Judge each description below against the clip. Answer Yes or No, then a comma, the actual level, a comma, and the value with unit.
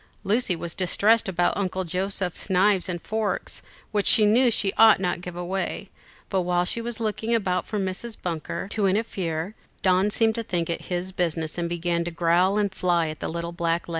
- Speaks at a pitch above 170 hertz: Yes, medium, 185 Hz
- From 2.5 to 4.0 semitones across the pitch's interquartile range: Yes, average, 3.2 semitones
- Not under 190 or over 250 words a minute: Yes, average, 200 wpm